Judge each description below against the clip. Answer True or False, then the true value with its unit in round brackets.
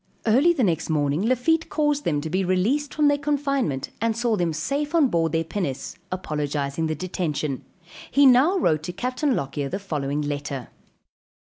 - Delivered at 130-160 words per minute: False (170 wpm)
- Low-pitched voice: False (185 Hz)